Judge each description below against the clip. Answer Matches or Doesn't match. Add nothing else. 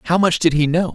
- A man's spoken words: Matches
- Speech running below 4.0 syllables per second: Doesn't match